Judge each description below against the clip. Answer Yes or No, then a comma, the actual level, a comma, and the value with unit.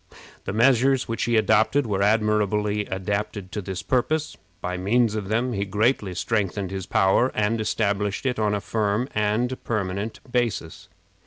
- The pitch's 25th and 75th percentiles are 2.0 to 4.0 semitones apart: Yes, narrow, 2.6 semitones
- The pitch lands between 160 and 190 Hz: No, low, 105 Hz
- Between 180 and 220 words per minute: No, average, 155 wpm